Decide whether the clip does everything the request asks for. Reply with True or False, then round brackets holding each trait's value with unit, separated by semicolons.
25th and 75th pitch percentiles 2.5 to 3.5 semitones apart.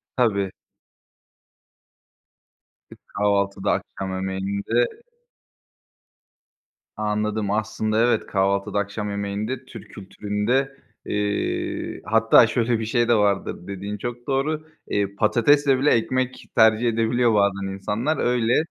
True (3.2 semitones)